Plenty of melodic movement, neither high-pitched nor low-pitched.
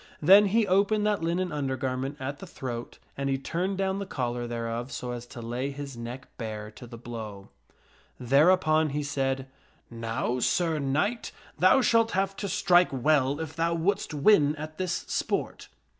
Yes: wide, 6.6 semitones; medium, 145 Hz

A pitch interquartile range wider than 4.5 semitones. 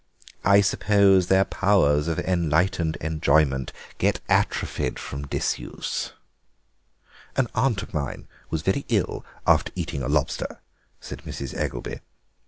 Yes: average, 5.0 semitones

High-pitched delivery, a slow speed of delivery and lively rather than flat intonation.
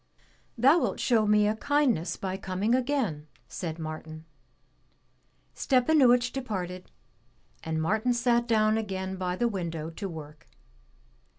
Yes: high, 210 Hz; slow, 120 wpm; wide, 5.9 semitones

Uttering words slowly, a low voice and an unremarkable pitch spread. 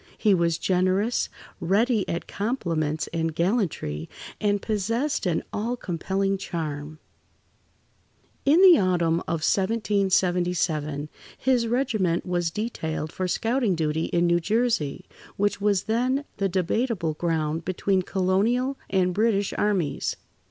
No: slow, 115 wpm; medium, 185 Hz; average, 4.7 semitones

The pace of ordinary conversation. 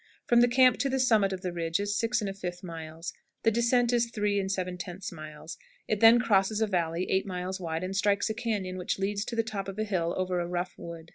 No: fast, 230 wpm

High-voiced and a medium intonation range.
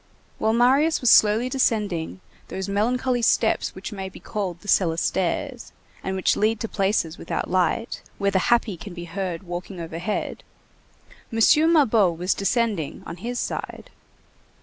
Yes: high, 205 Hz; average, 4.7 semitones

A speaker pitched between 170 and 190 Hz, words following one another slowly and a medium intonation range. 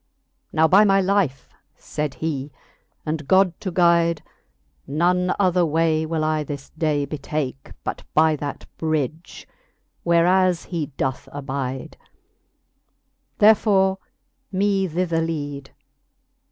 No: medium, 160 Hz; slow, 110 wpm; average, 3.8 semitones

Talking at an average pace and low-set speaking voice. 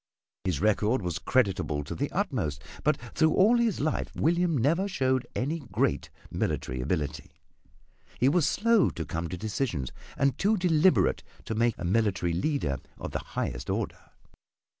Yes: average, 155 wpm; low, 130 Hz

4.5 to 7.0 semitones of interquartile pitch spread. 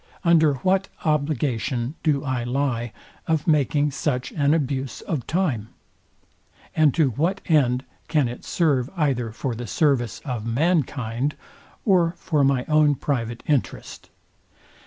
No: average, 4.0 semitones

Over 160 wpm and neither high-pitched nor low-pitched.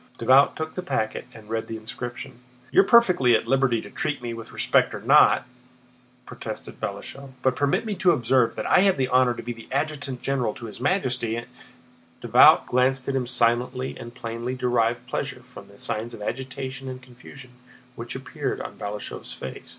No: average, 180 wpm; low, 125 Hz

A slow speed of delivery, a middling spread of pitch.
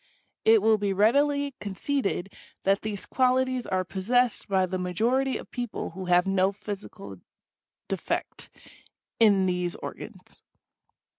Yes: slow, 125 wpm; average, 4.6 semitones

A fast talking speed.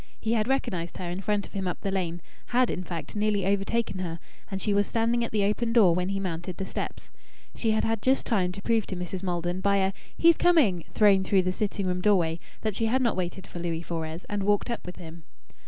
Yes: fast, 240 wpm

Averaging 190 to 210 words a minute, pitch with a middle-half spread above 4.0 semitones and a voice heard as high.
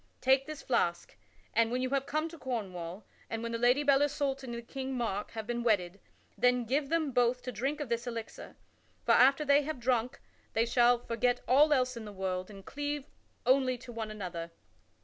No: average, 200 wpm; average, 3.2 semitones; high, 245 Hz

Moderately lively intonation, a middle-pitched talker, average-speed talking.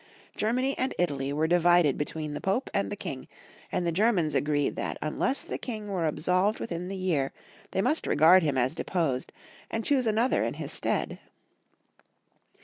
No: wide, 5.9 semitones; medium, 175 Hz; average, 170 wpm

